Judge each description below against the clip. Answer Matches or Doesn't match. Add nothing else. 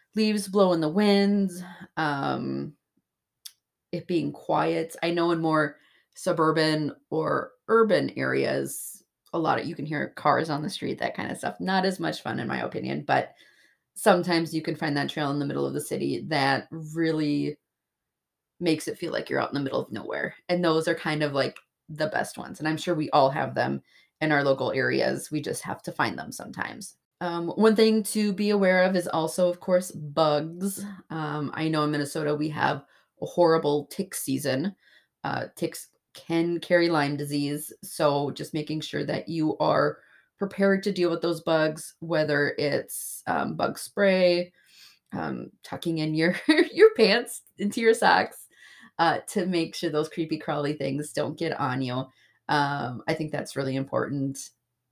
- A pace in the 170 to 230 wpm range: Matches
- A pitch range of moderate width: Matches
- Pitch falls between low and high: Matches